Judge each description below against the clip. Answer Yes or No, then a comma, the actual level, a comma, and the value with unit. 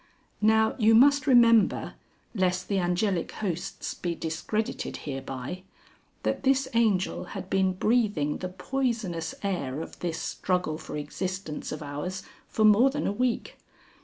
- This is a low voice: No, high, 190 Hz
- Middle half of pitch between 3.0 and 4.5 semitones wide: No, average, 4.9 semitones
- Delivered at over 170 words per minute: No, slow, 135 wpm